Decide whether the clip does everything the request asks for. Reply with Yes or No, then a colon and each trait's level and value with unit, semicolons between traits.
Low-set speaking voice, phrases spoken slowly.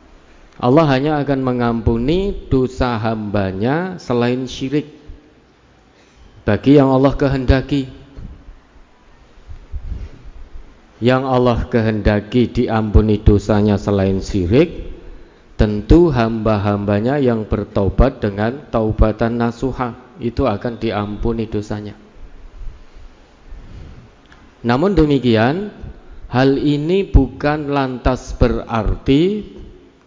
Yes: low, 115 Hz; slow, 75 wpm